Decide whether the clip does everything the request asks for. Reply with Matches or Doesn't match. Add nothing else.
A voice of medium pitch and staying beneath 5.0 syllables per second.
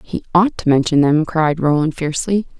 Doesn't match